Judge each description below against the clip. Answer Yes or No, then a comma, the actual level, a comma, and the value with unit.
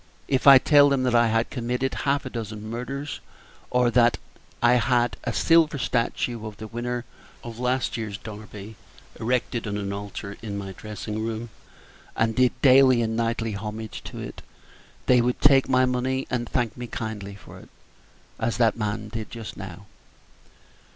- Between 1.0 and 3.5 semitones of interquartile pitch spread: Yes, narrow, 2.6 semitones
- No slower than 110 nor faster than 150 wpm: No, average, 170 wpm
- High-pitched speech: No, low, 115 Hz